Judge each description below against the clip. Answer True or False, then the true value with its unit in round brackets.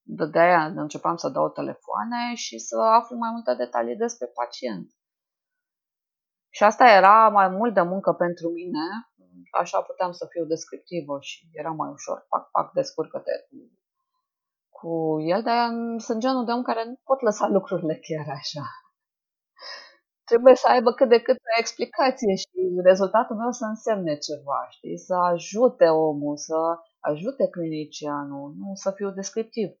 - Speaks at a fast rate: False (150 wpm)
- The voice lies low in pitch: False (195 Hz)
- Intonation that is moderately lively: False (6.7 semitones)